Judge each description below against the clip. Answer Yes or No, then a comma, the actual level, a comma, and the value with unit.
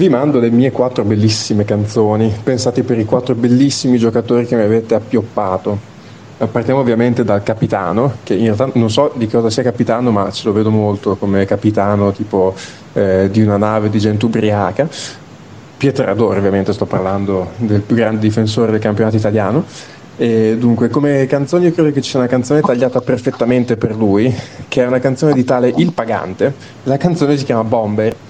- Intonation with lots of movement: No, average, 3.3 semitones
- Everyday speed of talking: No, fast, 180 wpm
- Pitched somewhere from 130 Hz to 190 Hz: No, low, 115 Hz